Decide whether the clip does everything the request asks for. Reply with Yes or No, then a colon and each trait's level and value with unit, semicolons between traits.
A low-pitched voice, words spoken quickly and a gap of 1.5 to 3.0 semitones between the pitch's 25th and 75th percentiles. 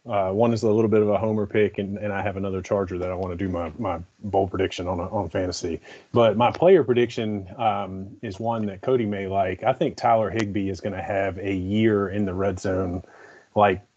Yes: low, 100 Hz; fast, 235 wpm; narrow, 2.4 semitones